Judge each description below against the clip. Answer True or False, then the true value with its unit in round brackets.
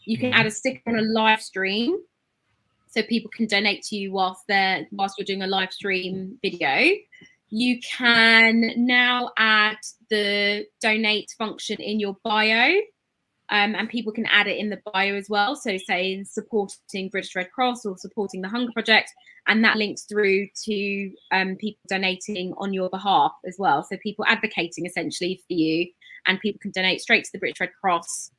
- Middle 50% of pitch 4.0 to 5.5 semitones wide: False (2.7 semitones)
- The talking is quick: False (180 wpm)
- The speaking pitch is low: False (210 Hz)